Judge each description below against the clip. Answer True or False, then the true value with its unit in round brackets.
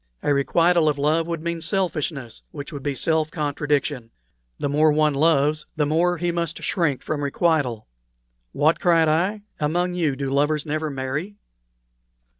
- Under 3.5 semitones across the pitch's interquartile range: True (2.7 semitones)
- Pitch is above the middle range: False (155 Hz)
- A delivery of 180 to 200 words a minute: False (155 wpm)